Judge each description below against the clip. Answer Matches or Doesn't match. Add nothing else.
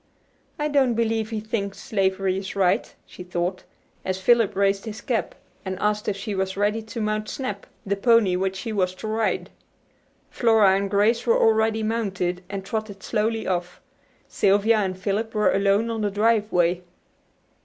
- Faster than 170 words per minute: Doesn't match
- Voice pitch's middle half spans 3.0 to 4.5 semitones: Doesn't match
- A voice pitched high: Matches